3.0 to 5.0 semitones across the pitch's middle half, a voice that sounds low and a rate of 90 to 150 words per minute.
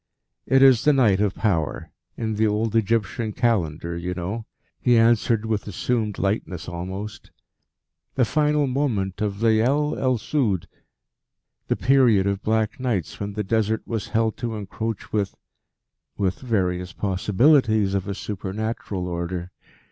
Yes: average, 3.3 semitones; low, 110 Hz; average, 140 wpm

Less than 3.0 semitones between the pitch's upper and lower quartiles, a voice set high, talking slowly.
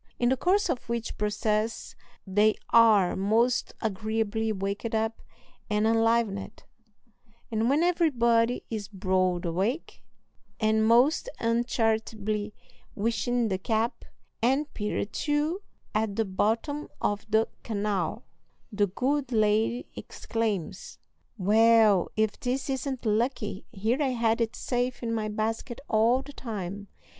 Yes: narrow, 2.5 semitones; high, 225 Hz; slow, 120 wpm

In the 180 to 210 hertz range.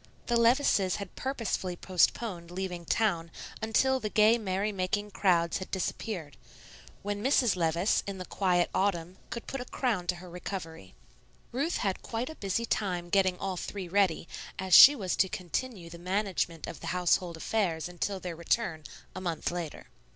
Yes: high, 190 Hz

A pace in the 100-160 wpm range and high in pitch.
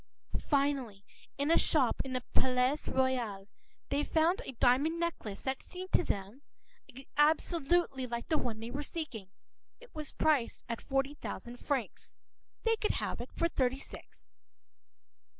Yes: average, 145 wpm; very high, 270 Hz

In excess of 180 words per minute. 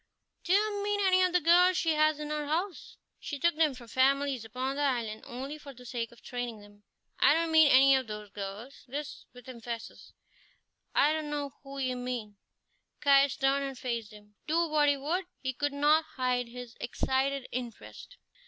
Yes: average, 190 wpm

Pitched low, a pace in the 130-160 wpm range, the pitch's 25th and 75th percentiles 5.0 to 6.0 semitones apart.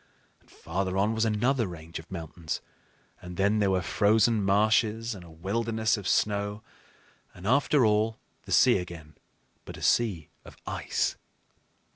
No: low, 105 Hz; average, 150 wpm; average, 3.8 semitones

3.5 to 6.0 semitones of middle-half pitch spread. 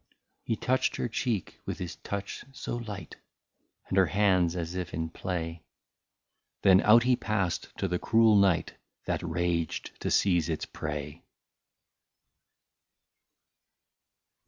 Yes: average, 3.9 semitones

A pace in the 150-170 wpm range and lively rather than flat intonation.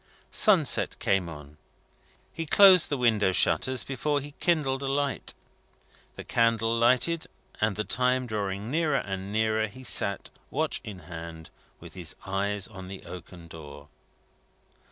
No: average, 140 wpm; wide, 6.0 semitones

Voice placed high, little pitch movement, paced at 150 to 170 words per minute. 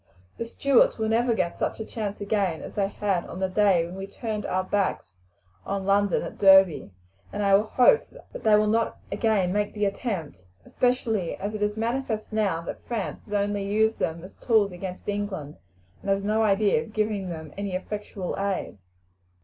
No: high, 205 Hz; narrow, 2.3 semitones; average, 190 wpm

